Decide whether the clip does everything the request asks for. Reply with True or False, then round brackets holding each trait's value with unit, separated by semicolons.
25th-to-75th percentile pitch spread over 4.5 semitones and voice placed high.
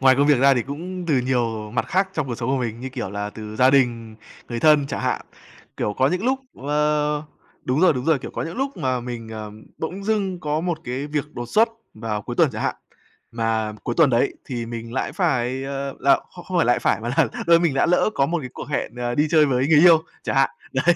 False (4.9 semitones; 135 Hz)